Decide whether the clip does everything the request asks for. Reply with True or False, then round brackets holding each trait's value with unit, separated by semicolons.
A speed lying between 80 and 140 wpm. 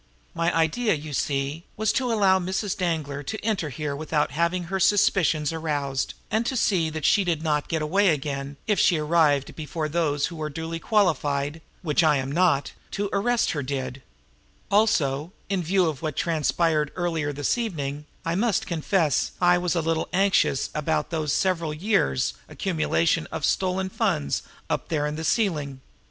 False (170 wpm)